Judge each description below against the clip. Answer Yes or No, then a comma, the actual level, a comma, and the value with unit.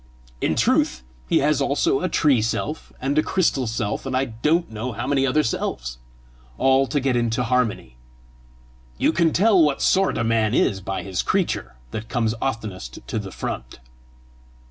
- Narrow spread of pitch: No, average, 4.8 semitones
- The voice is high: No, low, 125 Hz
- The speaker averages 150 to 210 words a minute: Yes, average, 170 wpm